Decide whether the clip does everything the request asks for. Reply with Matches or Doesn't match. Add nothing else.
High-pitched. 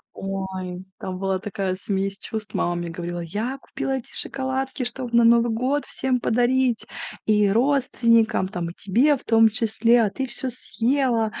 Matches